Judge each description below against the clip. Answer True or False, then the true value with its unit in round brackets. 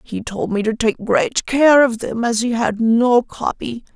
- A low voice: False (235 Hz)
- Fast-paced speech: True (210 wpm)